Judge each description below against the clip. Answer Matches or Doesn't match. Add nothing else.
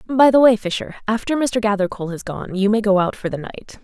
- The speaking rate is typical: Doesn't match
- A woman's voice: Matches